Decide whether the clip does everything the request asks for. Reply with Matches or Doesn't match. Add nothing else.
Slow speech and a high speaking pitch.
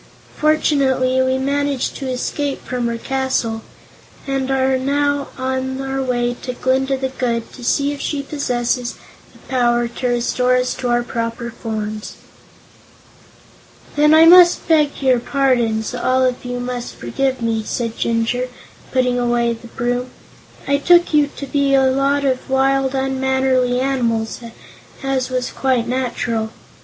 Doesn't match